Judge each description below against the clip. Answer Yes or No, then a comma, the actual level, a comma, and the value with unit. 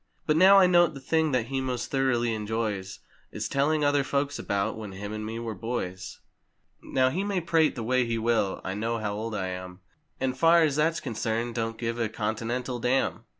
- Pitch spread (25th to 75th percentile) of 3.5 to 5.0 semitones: Yes, average, 4.3 semitones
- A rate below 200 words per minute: No, fast, 205 wpm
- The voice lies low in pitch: Yes, low, 120 Hz